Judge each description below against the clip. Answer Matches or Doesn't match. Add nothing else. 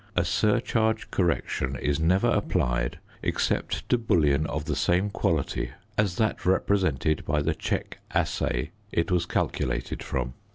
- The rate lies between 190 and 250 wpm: Doesn't match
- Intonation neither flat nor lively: Doesn't match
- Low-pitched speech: Matches